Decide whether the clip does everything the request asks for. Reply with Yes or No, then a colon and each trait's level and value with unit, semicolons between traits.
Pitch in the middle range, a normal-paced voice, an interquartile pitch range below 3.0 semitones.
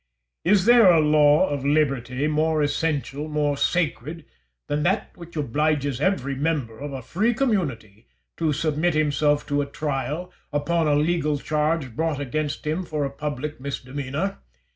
Yes: medium, 150 Hz; average, 150 wpm; narrow, 2.4 semitones